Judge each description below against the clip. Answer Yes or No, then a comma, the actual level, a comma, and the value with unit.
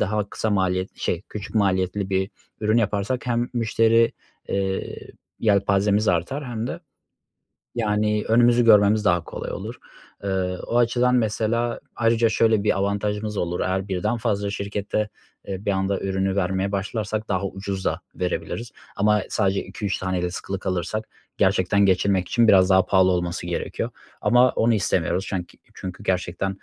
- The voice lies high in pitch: No, low, 100 Hz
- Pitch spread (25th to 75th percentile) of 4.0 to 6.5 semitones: No, narrow, 2.6 semitones